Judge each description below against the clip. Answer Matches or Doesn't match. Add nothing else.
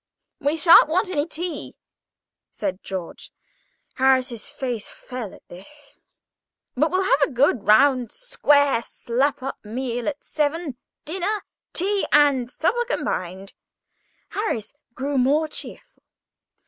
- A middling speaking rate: Doesn't match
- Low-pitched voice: Doesn't match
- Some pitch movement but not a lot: Matches